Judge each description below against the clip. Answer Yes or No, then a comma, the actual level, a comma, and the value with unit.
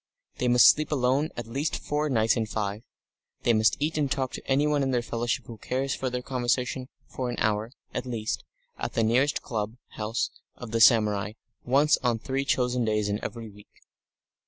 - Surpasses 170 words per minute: Yes, average, 200 wpm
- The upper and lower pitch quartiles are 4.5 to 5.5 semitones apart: No, average, 3.2 semitones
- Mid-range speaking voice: No, low, 120 Hz